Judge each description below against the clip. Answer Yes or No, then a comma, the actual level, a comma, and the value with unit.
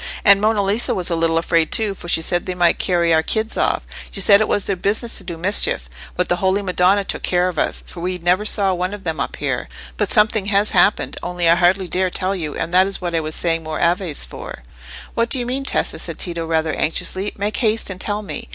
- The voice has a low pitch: No, medium, 185 Hz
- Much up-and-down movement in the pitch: No, average, 3.1 semitones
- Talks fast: Yes, fast, 250 wpm